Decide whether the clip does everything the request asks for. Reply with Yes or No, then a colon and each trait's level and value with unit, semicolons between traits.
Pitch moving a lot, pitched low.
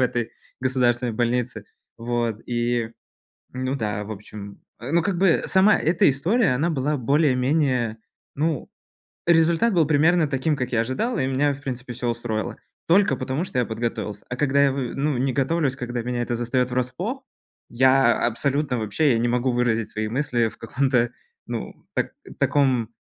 No: average, 3.5 semitones; low, 125 Hz